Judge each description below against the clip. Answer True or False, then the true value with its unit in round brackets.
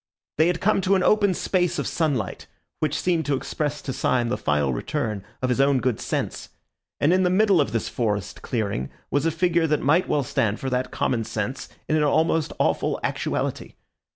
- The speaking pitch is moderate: True (145 Hz)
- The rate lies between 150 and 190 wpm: False (200 wpm)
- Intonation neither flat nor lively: False (5.9 semitones)